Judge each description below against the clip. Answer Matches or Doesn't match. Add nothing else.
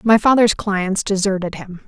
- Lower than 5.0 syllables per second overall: Doesn't match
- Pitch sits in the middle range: Doesn't match